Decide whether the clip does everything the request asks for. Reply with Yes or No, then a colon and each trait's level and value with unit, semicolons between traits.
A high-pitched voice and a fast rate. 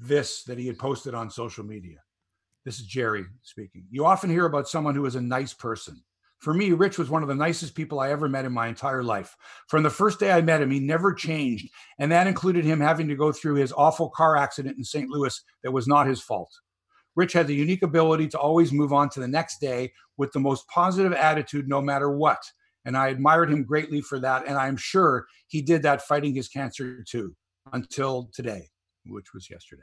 No: medium, 140 Hz; fast, 225 wpm